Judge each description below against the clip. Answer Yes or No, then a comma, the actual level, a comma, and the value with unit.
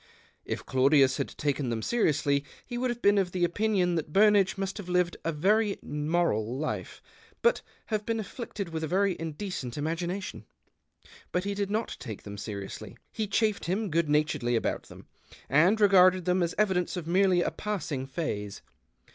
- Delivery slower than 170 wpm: No, average, 175 wpm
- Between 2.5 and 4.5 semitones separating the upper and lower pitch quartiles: No, average, 5.3 semitones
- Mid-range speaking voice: Yes, medium, 180 Hz